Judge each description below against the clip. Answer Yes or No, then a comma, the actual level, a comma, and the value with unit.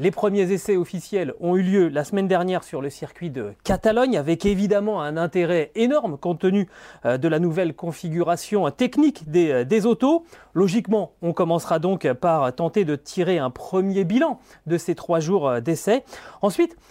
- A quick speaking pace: No, average, 165 wpm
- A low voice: No, medium, 185 Hz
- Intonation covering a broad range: No, average, 3.6 semitones